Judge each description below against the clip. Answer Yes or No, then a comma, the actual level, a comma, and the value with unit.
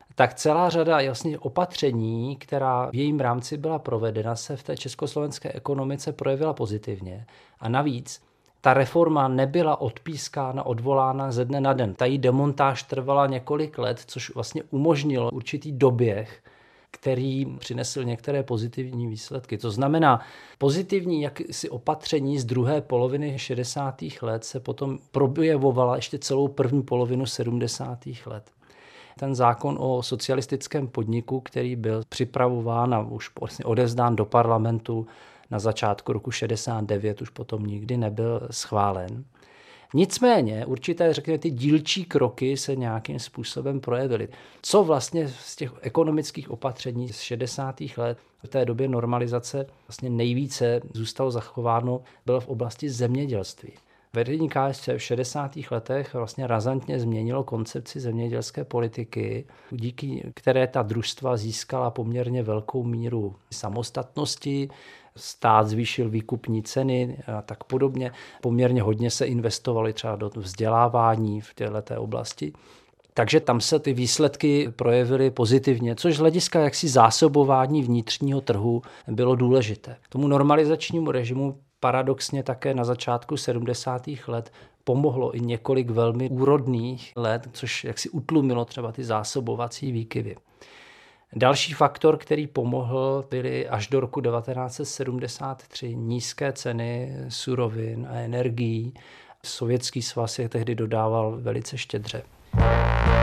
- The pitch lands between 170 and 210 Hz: No, low, 125 Hz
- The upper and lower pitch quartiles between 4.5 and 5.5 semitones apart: No, average, 2.8 semitones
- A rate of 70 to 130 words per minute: Yes, average, 125 wpm